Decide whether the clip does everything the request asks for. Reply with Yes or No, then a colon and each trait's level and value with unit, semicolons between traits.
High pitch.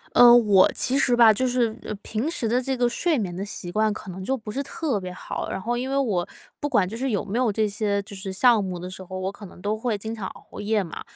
Yes: high, 215 Hz